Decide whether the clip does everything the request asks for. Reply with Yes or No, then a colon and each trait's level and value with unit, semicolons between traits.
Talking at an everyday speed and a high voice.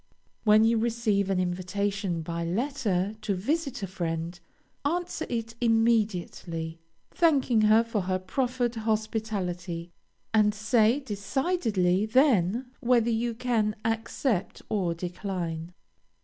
No: slow, 110 wpm; high, 215 Hz